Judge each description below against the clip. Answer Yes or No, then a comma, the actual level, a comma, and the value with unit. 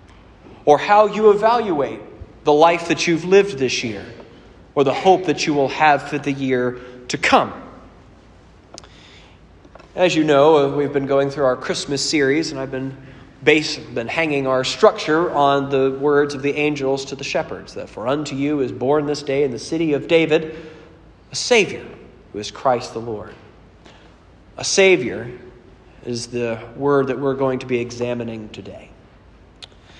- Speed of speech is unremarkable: Yes, average, 165 wpm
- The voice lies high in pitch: No, medium, 140 Hz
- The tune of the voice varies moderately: Yes, average, 3.8 semitones